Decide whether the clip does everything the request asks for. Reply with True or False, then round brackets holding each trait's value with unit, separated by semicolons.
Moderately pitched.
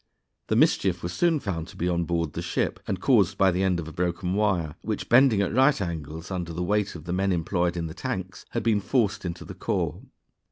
False (90 Hz)